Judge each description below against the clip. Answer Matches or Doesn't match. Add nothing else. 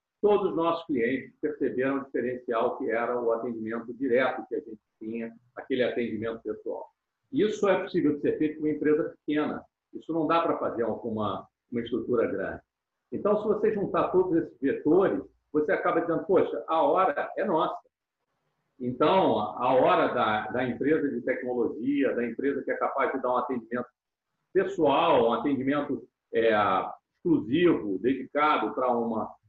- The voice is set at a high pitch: Doesn't match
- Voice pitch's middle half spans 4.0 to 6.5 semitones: Matches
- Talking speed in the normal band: Matches